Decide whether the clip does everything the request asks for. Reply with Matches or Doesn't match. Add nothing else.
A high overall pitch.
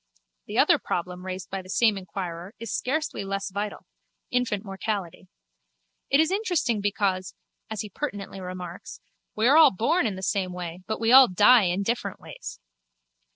Matches